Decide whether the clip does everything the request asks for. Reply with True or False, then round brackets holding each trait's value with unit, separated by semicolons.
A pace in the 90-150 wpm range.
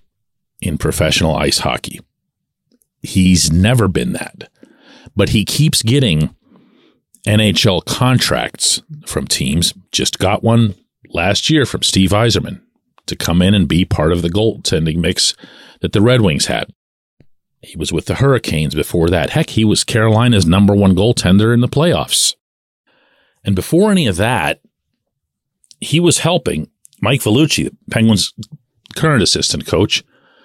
True (140 wpm)